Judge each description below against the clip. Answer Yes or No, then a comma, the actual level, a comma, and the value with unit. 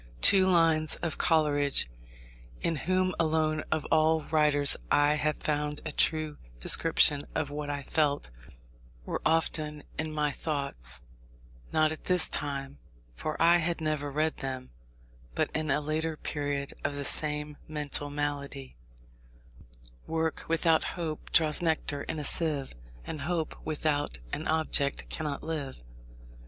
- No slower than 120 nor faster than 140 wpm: Yes, slow, 135 wpm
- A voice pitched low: No, medium, 150 Hz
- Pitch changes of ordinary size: No, narrow, 1.7 semitones